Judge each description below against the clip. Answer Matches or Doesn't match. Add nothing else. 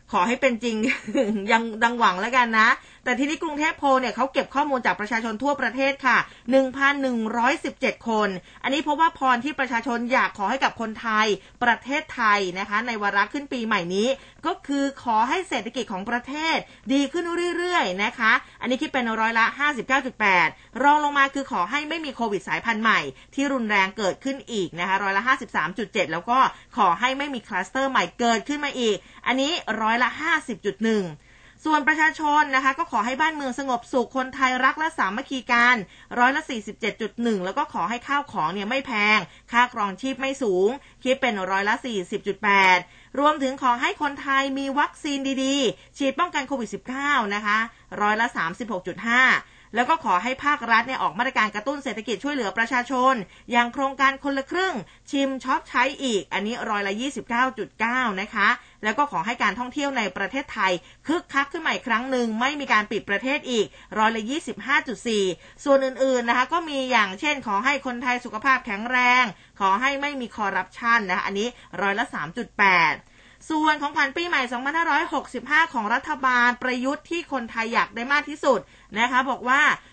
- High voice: Matches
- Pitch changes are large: Doesn't match